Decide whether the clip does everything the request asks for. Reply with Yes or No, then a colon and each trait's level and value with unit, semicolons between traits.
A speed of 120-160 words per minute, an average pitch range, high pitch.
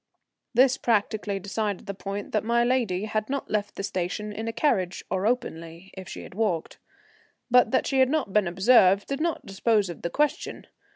No: average, 190 wpm; average, 4.0 semitones; high, 210 Hz